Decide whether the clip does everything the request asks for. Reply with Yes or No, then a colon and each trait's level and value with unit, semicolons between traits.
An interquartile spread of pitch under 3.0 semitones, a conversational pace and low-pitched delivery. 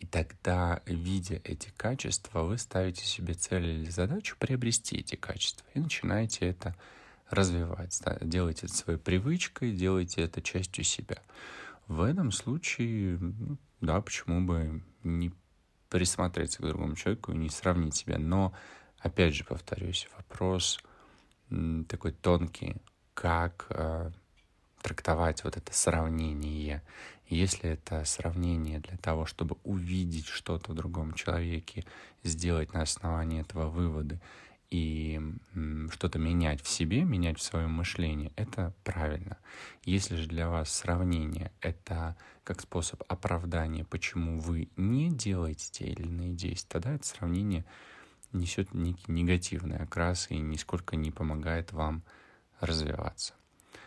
Yes: narrow, 2.5 semitones; average, 125 wpm; very low, 85 Hz